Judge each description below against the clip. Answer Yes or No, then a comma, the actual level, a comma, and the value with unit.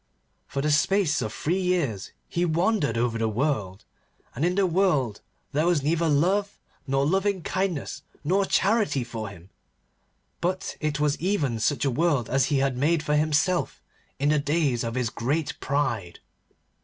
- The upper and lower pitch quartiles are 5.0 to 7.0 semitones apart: Yes, wide, 5.6 semitones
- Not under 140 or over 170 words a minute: Yes, average, 165 wpm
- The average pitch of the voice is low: No, medium, 150 Hz